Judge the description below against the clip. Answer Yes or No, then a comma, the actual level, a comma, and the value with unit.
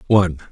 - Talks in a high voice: No, very low, 90 Hz